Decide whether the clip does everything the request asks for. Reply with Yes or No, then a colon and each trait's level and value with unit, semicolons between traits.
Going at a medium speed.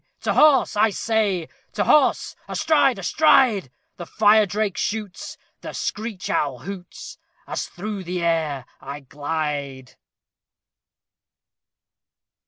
No: slow, 105 wpm